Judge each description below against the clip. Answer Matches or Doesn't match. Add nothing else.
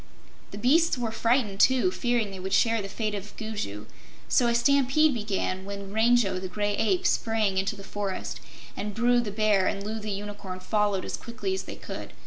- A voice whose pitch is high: Matches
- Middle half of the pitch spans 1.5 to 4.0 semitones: Matches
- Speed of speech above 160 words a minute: Matches